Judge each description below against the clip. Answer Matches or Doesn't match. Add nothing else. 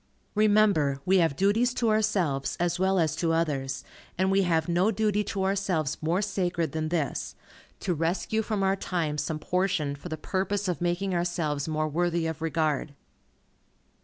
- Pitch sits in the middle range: Matches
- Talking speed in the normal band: Matches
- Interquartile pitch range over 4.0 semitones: Doesn't match